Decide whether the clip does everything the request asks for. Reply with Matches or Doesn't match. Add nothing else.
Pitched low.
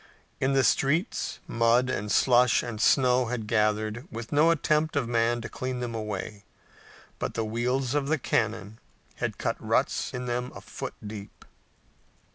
Matches